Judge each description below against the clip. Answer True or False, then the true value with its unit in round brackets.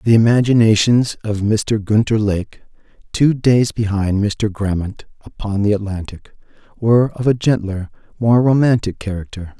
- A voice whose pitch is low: True (110 Hz)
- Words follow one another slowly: True (130 wpm)